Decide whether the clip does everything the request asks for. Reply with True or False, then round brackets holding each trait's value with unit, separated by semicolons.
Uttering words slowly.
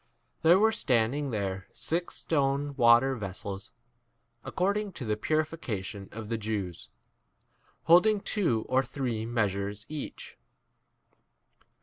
True (115 wpm)